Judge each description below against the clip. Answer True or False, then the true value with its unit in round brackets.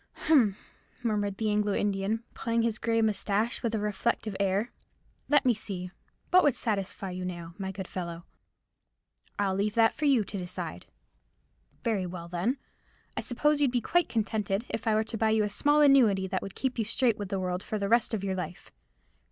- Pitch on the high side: True (210 Hz)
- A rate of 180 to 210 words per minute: True (195 wpm)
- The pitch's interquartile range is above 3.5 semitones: False (3.2 semitones)